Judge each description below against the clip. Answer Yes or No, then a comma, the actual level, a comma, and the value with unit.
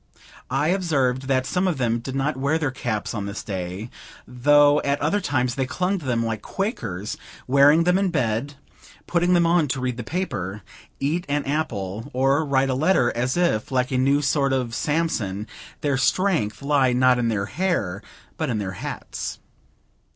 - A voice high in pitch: No, low, 135 Hz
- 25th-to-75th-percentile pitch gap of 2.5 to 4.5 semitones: No, average, 4.9 semitones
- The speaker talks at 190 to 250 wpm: No, average, 180 wpm